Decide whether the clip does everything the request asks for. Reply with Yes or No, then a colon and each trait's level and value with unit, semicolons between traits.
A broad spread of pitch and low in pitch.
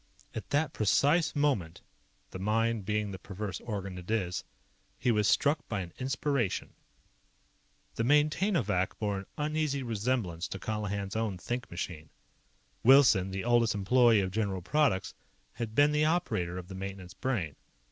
Yes: wide, 5.7 semitones; low, 110 Hz